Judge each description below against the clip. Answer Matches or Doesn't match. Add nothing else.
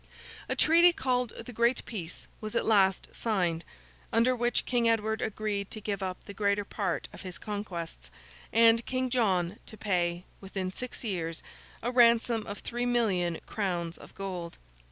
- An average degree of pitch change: Matches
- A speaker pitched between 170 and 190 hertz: Doesn't match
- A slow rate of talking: Doesn't match